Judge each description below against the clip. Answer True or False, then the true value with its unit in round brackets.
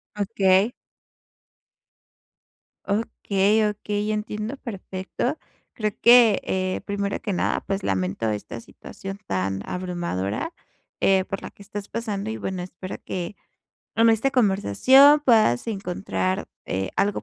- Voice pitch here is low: False (200 Hz)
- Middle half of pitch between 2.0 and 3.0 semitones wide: True (2.7 semitones)